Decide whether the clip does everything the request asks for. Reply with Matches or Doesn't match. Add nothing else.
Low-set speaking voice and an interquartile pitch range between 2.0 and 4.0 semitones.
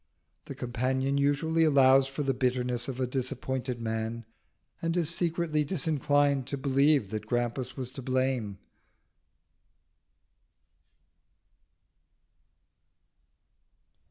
Matches